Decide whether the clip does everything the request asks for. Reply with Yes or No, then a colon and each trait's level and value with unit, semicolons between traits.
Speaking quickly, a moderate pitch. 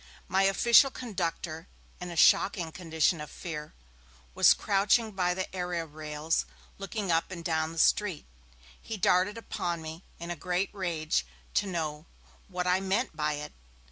No: average, 155 wpm; medium, 175 Hz